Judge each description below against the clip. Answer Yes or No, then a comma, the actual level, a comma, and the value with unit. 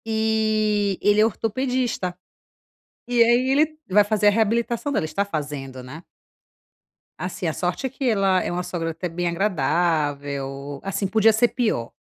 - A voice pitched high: Yes, high, 200 Hz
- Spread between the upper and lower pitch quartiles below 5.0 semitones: No, average, 5.3 semitones